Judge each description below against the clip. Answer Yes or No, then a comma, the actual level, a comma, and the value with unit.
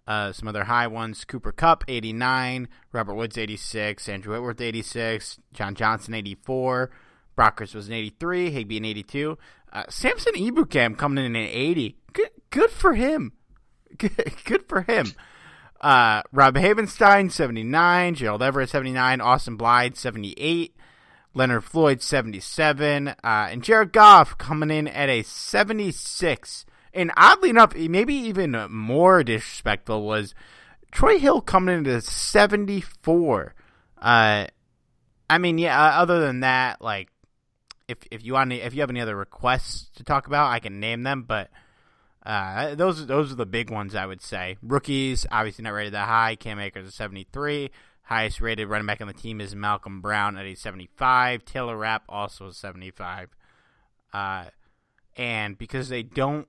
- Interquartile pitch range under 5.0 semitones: No, wide, 5.5 semitones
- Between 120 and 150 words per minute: No, average, 160 wpm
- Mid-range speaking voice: No, low, 120 Hz